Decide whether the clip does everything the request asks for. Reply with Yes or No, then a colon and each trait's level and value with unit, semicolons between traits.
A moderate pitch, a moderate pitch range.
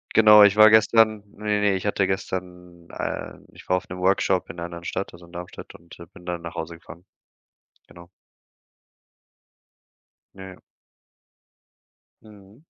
No: very low, 95 Hz; average, 3.0 semitones